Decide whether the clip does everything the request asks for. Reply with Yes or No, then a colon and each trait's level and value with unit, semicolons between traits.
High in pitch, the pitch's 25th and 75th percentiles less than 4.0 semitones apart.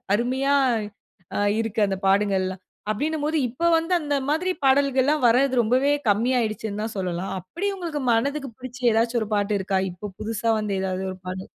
No: high, 230 Hz; wide, 5.4 semitones